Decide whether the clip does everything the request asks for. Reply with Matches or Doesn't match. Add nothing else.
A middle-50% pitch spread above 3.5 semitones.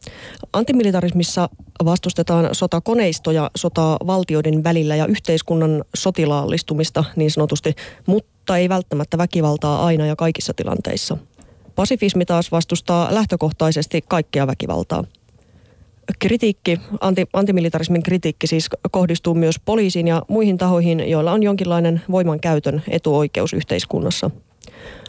Doesn't match